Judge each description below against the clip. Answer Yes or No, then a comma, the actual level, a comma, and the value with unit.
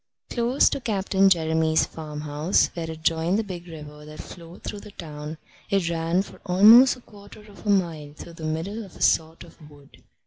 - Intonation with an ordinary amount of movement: Yes, average, 4.0 semitones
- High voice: No, medium, 170 Hz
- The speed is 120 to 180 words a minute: No, average, 195 wpm